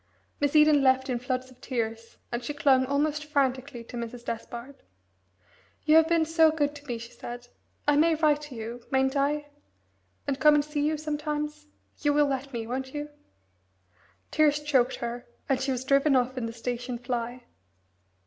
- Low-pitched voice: No, very high, 275 Hz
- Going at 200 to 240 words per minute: No, average, 180 wpm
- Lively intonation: No, average, 3.4 semitones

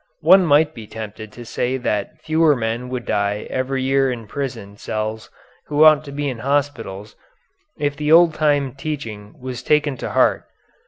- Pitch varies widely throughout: No, average, 4.7 semitones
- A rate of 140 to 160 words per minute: No, average, 170 wpm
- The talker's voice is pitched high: No, low, 130 Hz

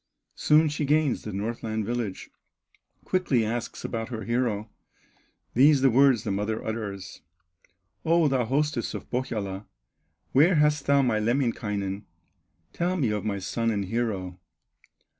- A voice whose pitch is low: Yes, low, 115 Hz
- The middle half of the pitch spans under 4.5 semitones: No, average, 4.8 semitones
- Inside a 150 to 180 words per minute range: No, slow, 135 wpm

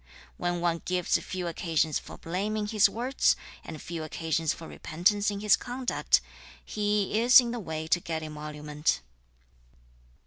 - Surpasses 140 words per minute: Yes, average, 150 wpm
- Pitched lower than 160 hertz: No, medium, 175 Hz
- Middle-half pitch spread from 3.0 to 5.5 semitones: Yes, average, 4.7 semitones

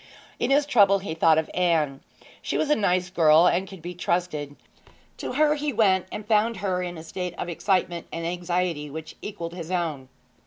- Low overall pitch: No, medium, 180 Hz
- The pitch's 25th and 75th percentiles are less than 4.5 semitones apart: Yes, average, 3.2 semitones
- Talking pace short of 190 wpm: No, average, 195 wpm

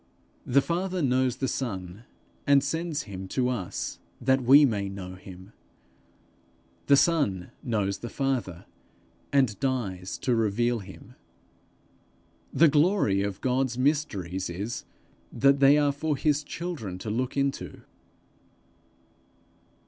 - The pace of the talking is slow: Yes, slow, 120 wpm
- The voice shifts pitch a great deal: Yes, wide, 6.1 semitones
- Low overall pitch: Yes, low, 125 Hz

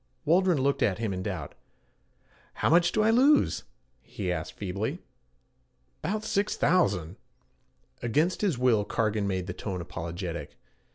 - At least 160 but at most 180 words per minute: No, slow, 135 wpm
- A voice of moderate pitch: No, low, 115 Hz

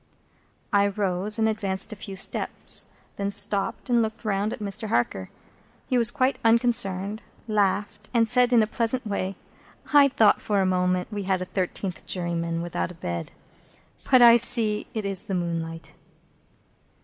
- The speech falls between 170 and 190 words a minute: No, average, 160 wpm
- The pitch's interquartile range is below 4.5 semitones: Yes, average, 3.5 semitones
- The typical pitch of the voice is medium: No, high, 205 Hz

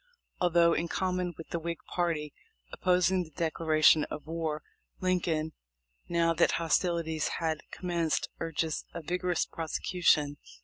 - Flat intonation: Yes, narrow, 1.8 semitones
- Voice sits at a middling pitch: Yes, medium, 165 Hz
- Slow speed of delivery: Yes, slow, 125 wpm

